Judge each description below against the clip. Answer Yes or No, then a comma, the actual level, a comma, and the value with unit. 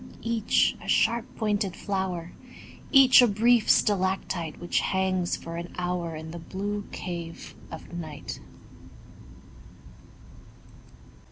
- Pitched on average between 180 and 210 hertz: Yes, high, 190 Hz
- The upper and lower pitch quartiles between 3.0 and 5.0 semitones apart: Yes, average, 3.5 semitones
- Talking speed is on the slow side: Yes, slow, 105 wpm